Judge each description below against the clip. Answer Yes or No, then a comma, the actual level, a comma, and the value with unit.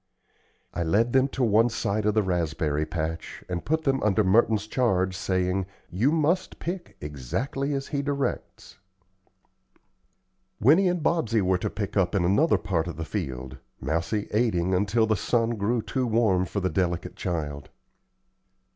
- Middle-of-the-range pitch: No, low, 100 Hz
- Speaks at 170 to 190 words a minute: No, average, 155 wpm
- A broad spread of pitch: Yes, wide, 5.8 semitones